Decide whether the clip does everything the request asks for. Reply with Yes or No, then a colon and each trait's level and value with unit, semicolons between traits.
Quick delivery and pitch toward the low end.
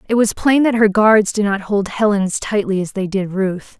No: fast, 255 wpm; high, 205 Hz